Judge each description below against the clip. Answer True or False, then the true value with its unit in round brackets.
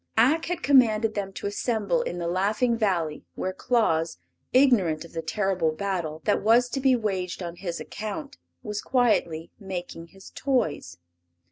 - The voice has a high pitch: True (200 Hz)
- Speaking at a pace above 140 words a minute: True (155 wpm)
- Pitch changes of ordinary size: False (5.8 semitones)